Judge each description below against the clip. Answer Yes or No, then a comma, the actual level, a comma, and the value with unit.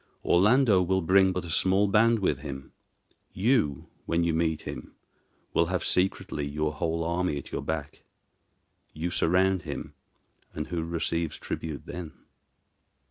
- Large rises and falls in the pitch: No, average, 3.3 semitones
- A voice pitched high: No, very low, 85 Hz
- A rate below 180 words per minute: Yes, average, 140 wpm